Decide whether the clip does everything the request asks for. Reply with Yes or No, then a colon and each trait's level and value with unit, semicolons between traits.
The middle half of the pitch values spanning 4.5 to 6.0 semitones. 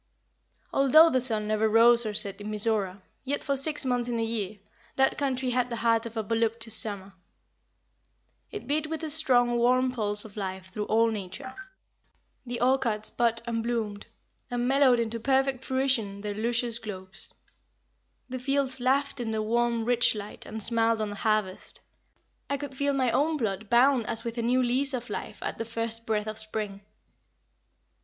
No: average, 3.1 semitones